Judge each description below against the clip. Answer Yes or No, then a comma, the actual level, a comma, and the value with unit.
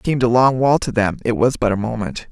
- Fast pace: Yes, fast, 285 wpm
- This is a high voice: No, low, 135 Hz